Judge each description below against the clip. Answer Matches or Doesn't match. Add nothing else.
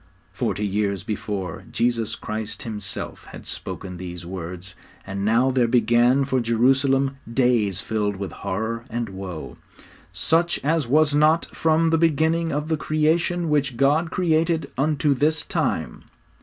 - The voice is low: Matches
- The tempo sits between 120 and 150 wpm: Matches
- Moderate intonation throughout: Doesn't match